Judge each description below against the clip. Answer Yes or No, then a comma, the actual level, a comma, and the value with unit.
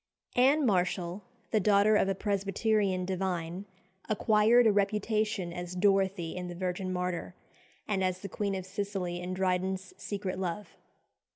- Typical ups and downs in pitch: No, narrow, 2.3 semitones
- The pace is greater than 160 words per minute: No, average, 145 wpm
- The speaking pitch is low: No, high, 190 Hz